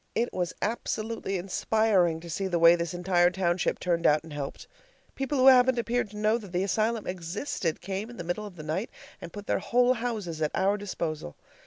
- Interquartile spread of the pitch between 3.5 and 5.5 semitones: Yes, average, 4.4 semitones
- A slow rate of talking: No, fast, 205 wpm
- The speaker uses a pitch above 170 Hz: Yes, high, 190 Hz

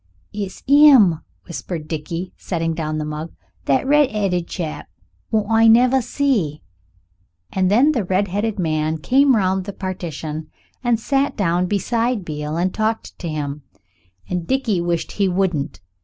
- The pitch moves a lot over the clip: Yes, wide, 5.7 semitones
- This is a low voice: No, medium, 185 Hz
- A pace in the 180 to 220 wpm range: No, average, 140 wpm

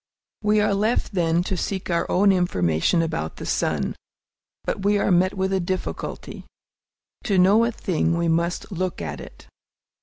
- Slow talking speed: No, average, 170 wpm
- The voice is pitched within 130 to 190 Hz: Yes, medium, 185 Hz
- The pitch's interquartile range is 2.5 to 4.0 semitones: Yes, average, 2.8 semitones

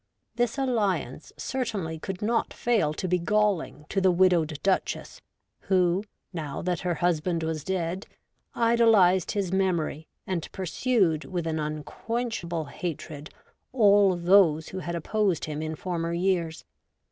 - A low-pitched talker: No, medium, 180 Hz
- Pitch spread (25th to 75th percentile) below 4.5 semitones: Yes, average, 3.7 semitones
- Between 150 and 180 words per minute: No, slow, 135 wpm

